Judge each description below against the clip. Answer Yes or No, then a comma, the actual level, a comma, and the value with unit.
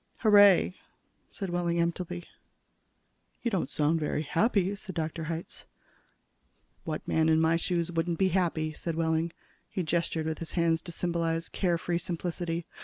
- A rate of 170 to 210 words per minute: No, average, 150 wpm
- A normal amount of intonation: No, narrow, 1.6 semitones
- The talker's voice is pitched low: No, medium, 170 Hz